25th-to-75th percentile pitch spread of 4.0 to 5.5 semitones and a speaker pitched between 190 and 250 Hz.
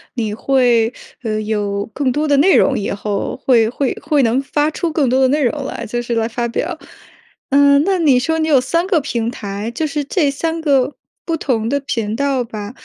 No: average, 4.3 semitones; very high, 260 Hz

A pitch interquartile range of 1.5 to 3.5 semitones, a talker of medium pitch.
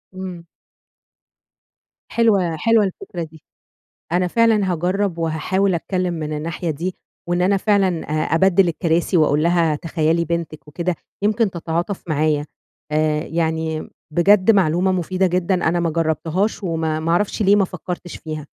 Yes: average, 2.9 semitones; medium, 170 Hz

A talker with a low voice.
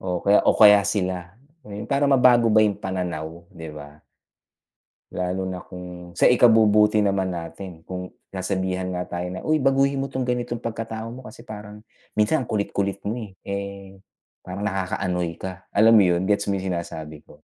Yes: low, 100 Hz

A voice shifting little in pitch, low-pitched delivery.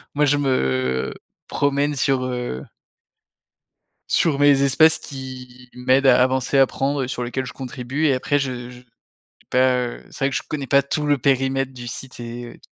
Yes: narrow, 2.0 semitones; low, 130 Hz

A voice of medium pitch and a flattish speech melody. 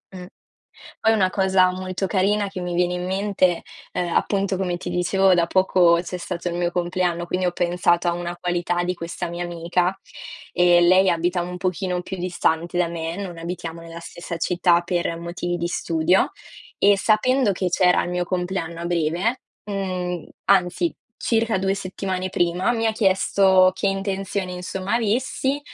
Yes: medium, 180 Hz; narrow, 1.7 semitones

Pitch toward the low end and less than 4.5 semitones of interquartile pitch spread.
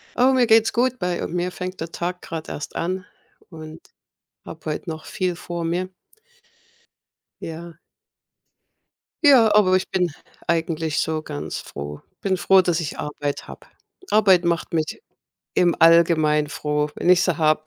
No: medium, 170 Hz; average, 2.8 semitones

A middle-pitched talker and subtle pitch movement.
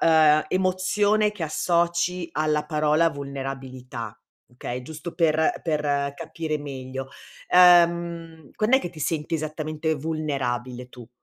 No: medium, 155 Hz; average, 3.5 semitones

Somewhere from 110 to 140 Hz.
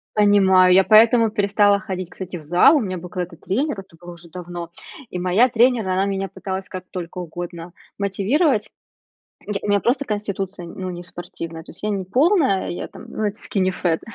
No: high, 190 Hz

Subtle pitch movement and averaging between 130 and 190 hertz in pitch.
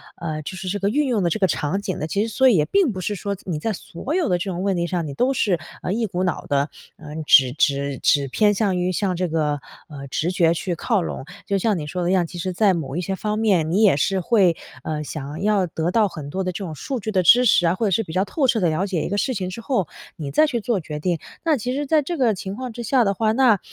No: average, 4.8 semitones; medium, 185 Hz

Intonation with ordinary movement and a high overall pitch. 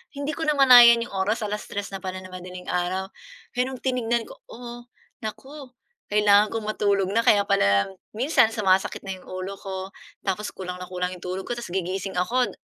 Yes: average, 4.2 semitones; high, 200 Hz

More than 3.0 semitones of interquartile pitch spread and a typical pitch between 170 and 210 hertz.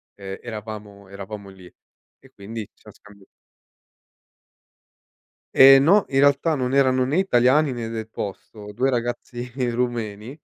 No: average, 4.3 semitones; low, 120 Hz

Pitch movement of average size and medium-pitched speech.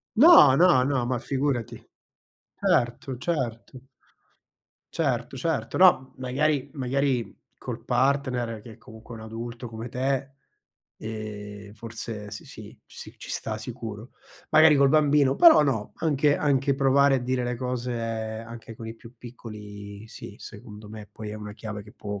No: average, 3.7 semitones; low, 120 Hz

